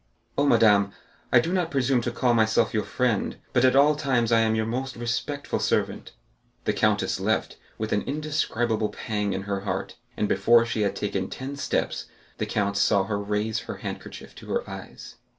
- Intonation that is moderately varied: Yes, average, 4.0 semitones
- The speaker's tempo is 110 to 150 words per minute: No, average, 185 wpm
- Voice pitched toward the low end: Yes, low, 115 Hz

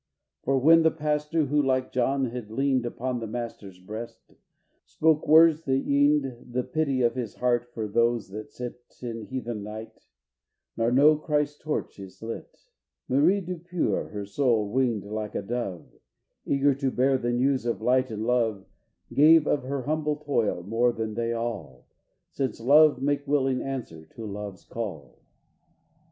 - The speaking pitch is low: Yes, low, 125 Hz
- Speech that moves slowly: No, average, 160 wpm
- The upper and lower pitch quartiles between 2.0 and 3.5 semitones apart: No, average, 4.1 semitones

